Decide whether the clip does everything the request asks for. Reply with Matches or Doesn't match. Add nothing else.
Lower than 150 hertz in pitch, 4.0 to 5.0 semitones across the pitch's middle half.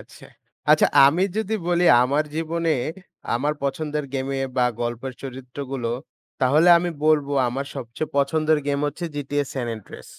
Doesn't match